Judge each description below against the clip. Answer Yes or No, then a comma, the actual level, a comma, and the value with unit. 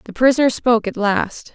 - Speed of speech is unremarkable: Yes, average, 195 wpm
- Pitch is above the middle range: Yes, high, 230 Hz